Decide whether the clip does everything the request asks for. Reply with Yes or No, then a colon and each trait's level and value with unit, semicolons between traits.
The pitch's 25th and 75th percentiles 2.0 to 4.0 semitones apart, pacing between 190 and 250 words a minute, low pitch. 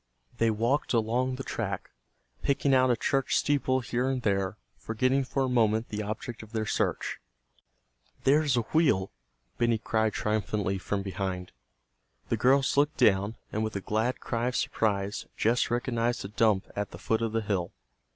No: average, 3.6 semitones; average, 170 wpm; low, 115 Hz